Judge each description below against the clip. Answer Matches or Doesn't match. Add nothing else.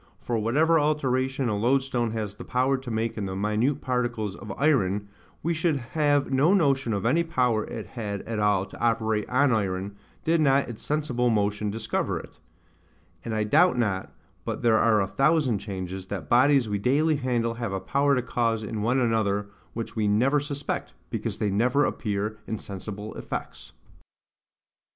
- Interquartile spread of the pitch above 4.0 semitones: Matches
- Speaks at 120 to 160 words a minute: Doesn't match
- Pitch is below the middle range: Matches